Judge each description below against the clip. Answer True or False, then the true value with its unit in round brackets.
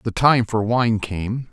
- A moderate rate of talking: True (195 wpm)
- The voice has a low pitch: True (110 Hz)